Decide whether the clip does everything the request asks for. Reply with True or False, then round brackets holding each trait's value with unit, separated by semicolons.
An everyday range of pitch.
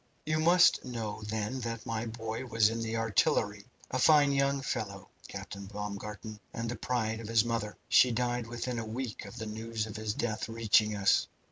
False (2.1 semitones)